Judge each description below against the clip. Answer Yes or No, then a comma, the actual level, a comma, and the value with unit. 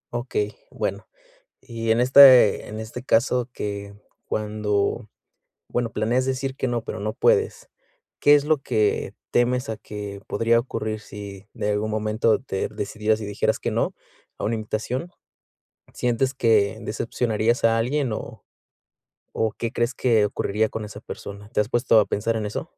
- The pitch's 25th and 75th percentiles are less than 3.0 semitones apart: Yes, narrow, 2.6 semitones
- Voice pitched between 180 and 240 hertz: No, low, 110 Hz